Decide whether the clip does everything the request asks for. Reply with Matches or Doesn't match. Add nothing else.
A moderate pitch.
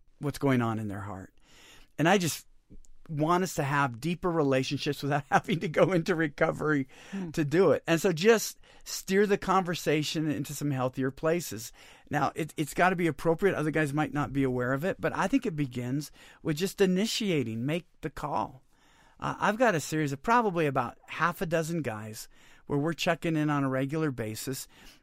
Matches